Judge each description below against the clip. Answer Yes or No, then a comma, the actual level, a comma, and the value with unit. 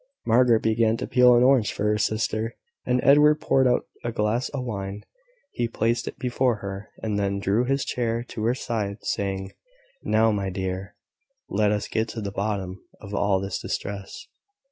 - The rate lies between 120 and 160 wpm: No, average, 180 wpm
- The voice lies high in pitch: No, low, 110 Hz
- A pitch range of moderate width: Yes, average, 3.2 semitones